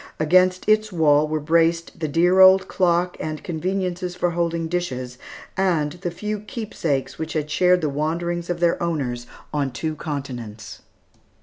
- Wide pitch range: No, average, 3.2 semitones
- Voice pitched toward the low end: No, medium, 170 Hz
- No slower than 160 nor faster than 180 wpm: No, average, 150 wpm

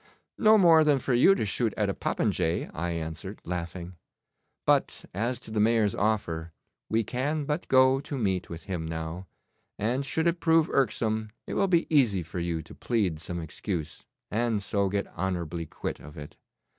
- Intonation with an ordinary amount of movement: No, wide, 7.3 semitones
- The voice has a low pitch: Yes, low, 105 Hz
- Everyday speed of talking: Yes, average, 180 wpm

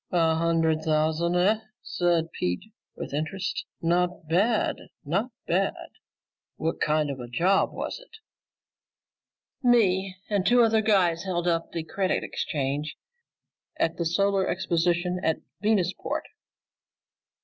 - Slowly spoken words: Yes, slow, 120 wpm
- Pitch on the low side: No, medium, 175 Hz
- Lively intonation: No, average, 3.3 semitones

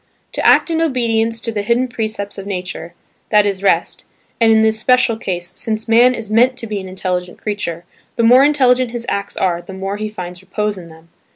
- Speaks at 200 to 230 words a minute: Yes, fast, 205 wpm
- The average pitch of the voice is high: Yes, high, 215 Hz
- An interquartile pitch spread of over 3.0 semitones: Yes, average, 3.7 semitones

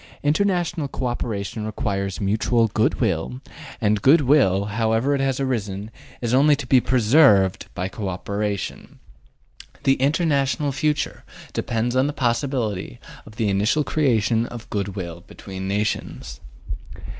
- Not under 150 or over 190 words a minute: No, slow, 135 wpm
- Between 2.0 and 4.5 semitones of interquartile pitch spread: No, average, 5.3 semitones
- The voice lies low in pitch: Yes, low, 115 Hz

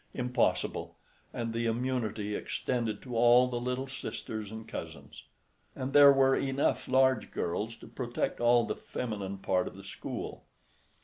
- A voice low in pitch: Yes, low, 120 Hz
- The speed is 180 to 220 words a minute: No, average, 140 wpm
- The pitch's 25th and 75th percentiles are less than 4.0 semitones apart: Yes, average, 2.8 semitones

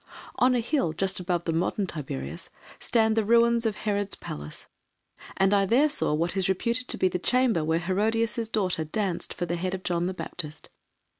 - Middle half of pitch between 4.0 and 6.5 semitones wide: Yes, average, 4.7 semitones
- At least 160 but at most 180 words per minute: No, average, 195 wpm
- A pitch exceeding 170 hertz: Yes, high, 190 Hz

